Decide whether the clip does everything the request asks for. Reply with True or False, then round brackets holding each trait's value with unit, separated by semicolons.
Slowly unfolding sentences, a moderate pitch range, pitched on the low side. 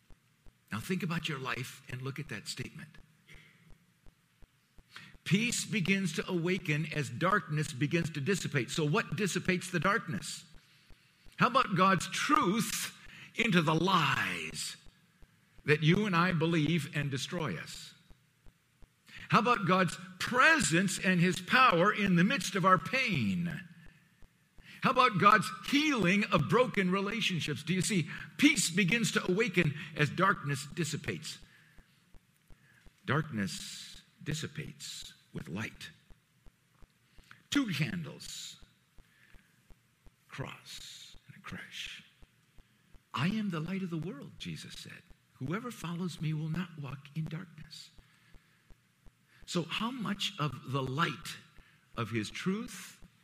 False (120 wpm; 3.7 semitones; 170 Hz)